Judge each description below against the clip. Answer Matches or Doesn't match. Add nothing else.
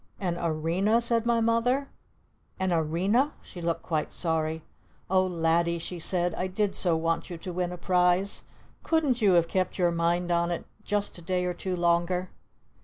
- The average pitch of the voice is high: Doesn't match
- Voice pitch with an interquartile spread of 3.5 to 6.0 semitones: Doesn't match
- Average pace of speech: Matches